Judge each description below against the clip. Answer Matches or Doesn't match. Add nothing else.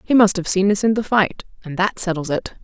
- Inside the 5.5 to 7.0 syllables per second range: Matches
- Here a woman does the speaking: Matches